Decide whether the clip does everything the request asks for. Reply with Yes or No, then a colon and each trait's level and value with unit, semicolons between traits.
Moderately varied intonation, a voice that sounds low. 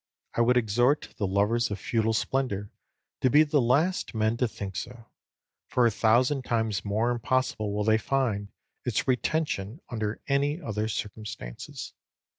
Yes: average, 3.4 semitones; low, 115 Hz